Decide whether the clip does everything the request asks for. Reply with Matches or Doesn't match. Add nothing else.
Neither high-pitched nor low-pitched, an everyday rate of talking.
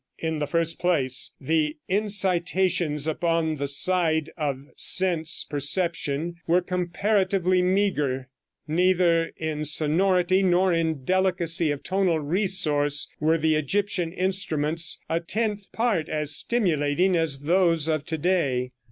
Doesn't match